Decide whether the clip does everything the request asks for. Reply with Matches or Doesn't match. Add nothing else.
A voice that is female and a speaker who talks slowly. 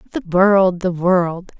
Matches